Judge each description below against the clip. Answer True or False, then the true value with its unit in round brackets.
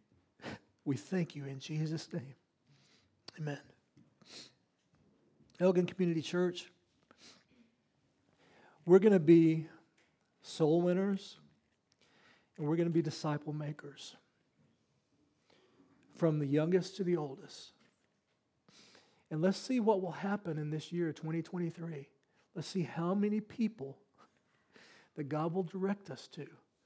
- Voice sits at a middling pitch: True (165 Hz)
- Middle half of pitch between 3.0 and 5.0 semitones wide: True (3.4 semitones)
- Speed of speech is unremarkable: False (110 wpm)